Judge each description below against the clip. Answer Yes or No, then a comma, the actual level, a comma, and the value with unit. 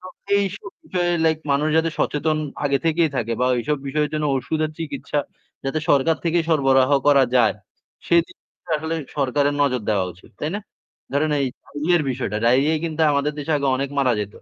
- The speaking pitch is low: No, medium, 145 Hz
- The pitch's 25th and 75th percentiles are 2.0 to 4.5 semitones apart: Yes, average, 3.0 semitones